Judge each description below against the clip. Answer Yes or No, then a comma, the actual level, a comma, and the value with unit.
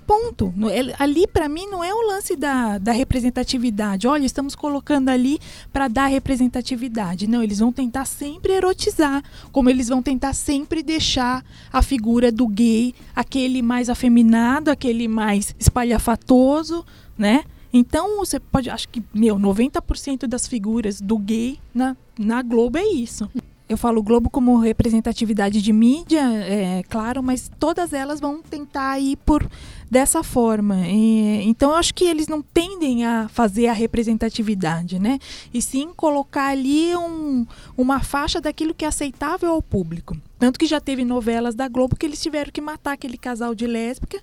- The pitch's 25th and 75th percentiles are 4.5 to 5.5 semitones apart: No, average, 4.1 semitones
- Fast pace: No, average, 160 wpm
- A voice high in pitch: Yes, very high, 255 Hz